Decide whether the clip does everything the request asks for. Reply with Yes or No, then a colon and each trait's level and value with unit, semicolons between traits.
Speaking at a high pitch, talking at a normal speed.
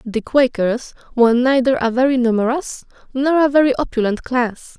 Yes: very high, 250 Hz; average, 150 wpm